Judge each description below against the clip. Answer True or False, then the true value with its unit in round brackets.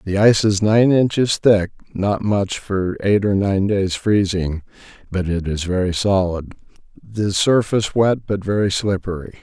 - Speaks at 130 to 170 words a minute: True (155 wpm)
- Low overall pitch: True (100 Hz)